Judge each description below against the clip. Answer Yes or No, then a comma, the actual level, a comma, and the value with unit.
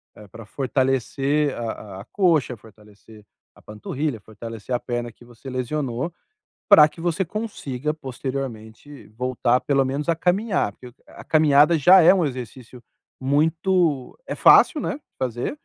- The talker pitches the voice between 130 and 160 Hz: Yes, low, 135 Hz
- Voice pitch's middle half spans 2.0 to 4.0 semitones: No, average, 4.7 semitones